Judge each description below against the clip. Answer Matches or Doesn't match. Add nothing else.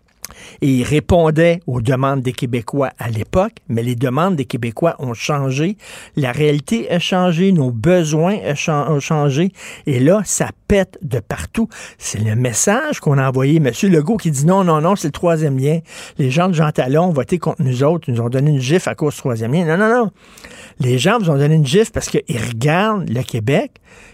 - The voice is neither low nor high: Matches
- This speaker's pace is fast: Doesn't match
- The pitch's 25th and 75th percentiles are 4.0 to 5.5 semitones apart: Matches